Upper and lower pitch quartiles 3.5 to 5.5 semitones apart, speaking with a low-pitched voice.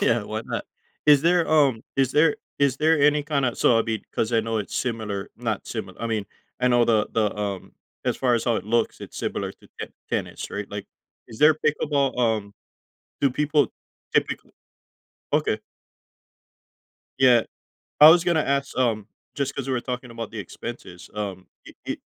Yes: average, 4.4 semitones; low, 120 Hz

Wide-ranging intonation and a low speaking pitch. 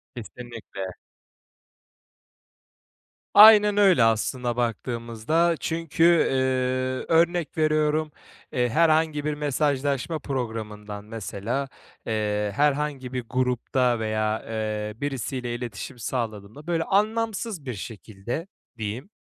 Yes: wide, 5.8 semitones; low, 125 Hz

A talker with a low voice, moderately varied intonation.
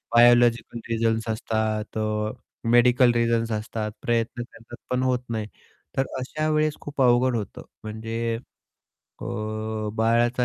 No: low, 115 Hz; narrow, 1.7 semitones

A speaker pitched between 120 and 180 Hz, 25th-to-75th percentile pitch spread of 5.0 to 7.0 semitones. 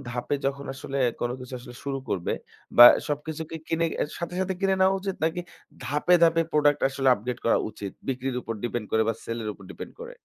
Yes: medium, 140 Hz; wide, 5.4 semitones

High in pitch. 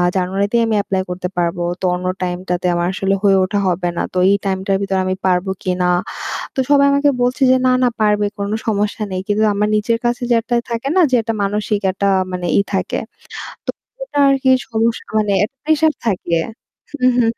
Yes: high, 205 Hz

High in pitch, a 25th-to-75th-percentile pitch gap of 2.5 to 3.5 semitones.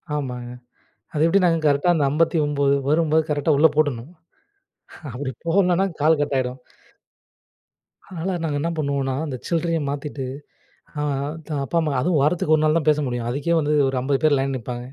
No: medium, 150 Hz; average, 2.9 semitones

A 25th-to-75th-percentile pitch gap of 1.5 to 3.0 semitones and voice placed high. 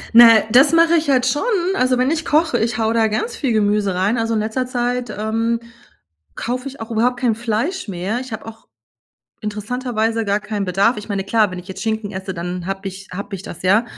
No: average, 3.6 semitones; high, 225 Hz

